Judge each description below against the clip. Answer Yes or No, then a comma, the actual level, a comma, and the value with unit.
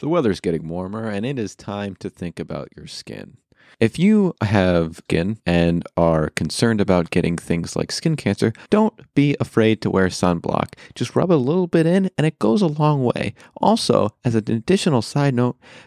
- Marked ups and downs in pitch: Yes, wide, 8.6 semitones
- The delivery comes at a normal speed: Yes, average, 190 wpm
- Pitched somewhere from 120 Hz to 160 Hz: No, low, 110 Hz